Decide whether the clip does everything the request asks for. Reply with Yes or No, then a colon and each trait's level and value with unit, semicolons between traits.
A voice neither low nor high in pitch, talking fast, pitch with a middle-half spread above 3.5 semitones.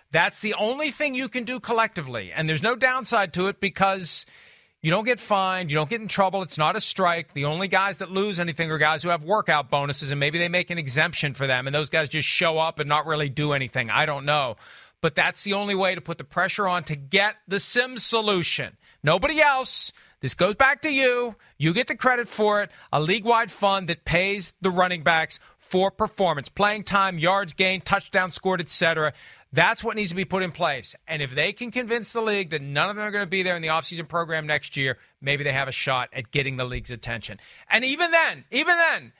Yes: medium, 180 Hz; fast, 235 wpm; wide, 5.4 semitones